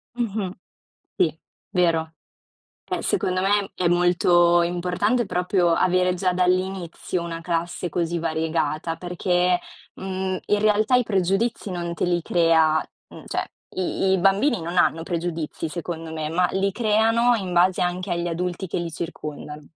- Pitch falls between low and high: Yes, medium, 180 Hz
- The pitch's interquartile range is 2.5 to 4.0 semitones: No, narrow, 2.1 semitones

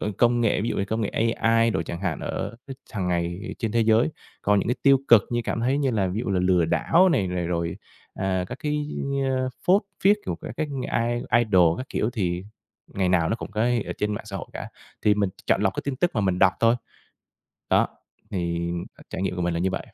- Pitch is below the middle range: Yes, low, 105 Hz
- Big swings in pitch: No, average, 4.7 semitones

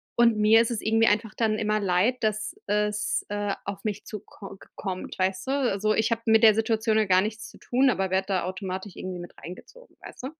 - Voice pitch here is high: Yes, high, 210 Hz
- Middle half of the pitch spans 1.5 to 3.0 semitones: Yes, narrow, 2.5 semitones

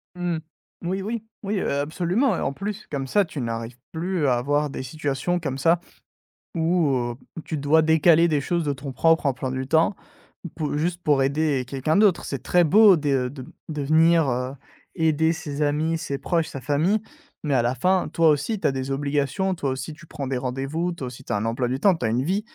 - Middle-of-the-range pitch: Yes, medium, 150 Hz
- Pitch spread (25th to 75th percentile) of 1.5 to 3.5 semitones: No, average, 4.1 semitones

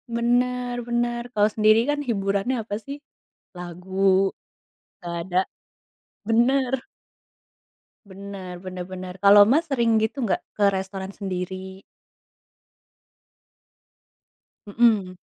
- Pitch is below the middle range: No, high, 200 Hz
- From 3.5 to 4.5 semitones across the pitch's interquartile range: Yes, average, 4.0 semitones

